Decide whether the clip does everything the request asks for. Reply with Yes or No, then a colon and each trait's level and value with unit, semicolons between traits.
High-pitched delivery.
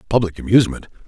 No: low, 105 Hz